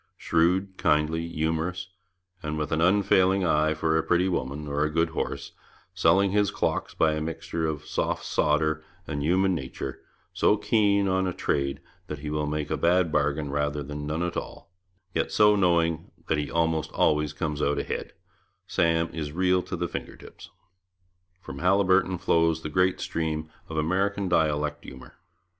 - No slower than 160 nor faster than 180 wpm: Yes, average, 165 wpm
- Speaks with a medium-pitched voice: No, very low, 80 Hz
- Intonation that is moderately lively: Yes, average, 3.3 semitones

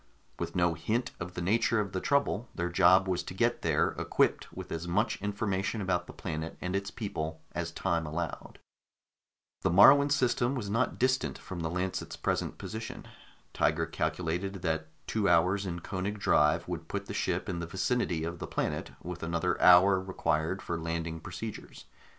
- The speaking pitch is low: Yes, very low, 90 Hz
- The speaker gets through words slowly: No, average, 175 wpm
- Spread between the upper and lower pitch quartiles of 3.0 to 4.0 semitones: Yes, average, 3.3 semitones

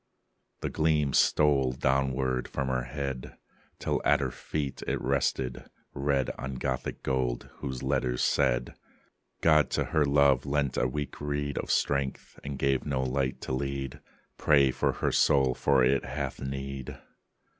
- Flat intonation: Yes, narrow, 1.6 semitones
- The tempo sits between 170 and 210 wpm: No, average, 150 wpm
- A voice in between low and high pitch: No, very low, 65 Hz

